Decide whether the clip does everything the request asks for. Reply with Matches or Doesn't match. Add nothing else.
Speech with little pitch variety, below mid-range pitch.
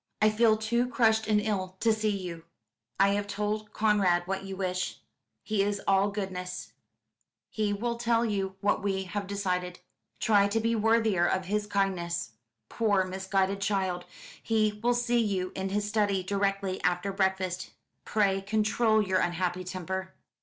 Doesn't match